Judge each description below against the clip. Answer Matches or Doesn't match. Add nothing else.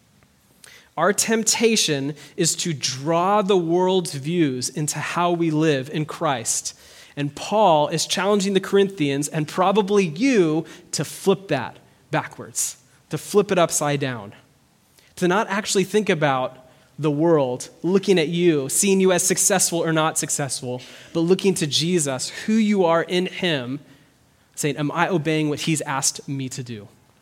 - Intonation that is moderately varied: Matches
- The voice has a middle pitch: Matches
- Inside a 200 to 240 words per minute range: Doesn't match